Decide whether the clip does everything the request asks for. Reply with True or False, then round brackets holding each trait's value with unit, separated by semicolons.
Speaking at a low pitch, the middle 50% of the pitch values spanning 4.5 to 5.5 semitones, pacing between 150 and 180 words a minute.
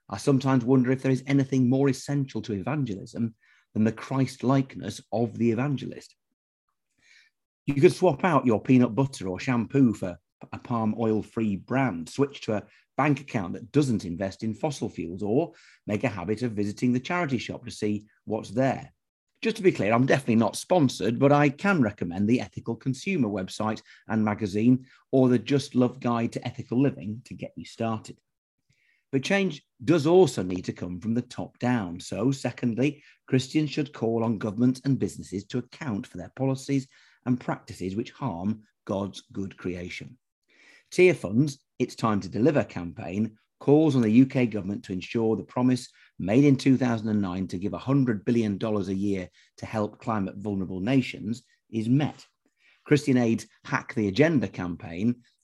False (120 Hz; 4.1 semitones; 170 wpm)